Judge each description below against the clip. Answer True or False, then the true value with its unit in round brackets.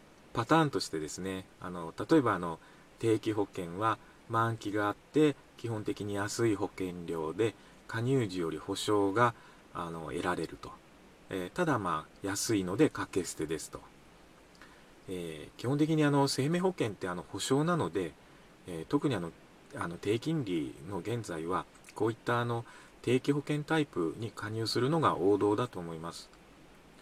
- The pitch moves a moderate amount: False (6.9 semitones)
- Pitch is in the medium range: False (110 Hz)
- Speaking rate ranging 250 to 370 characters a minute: True (290 characters per minute)